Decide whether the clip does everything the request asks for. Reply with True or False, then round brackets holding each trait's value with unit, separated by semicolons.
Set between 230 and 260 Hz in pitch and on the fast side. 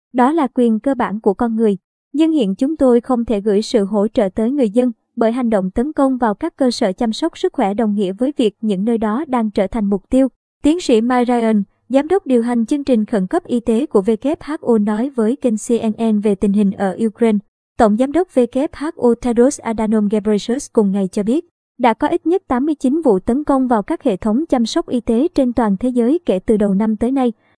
False (240 Hz; 235 wpm)